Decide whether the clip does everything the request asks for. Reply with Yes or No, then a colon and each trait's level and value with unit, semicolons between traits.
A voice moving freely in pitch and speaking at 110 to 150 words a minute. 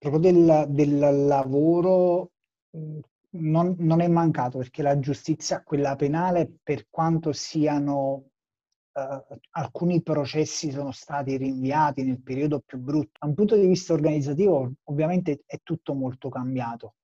No: average, 2.8 semitones; average, 130 wpm